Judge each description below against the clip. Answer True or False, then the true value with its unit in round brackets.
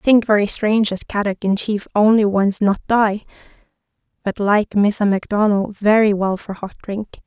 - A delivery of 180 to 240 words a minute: False (165 wpm)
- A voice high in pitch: True (205 Hz)